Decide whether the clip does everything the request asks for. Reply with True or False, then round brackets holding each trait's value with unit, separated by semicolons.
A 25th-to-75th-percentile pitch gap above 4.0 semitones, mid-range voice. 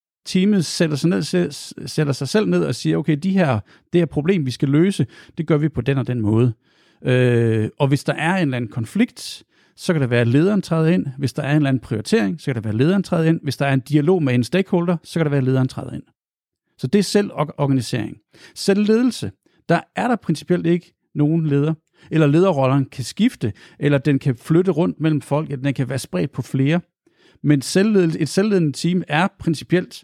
True (4.7 semitones; 155 Hz)